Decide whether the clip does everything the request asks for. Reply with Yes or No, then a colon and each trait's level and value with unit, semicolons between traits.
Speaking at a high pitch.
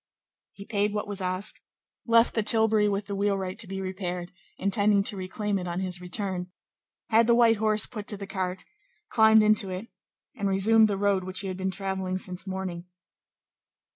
Yes: high, 200 Hz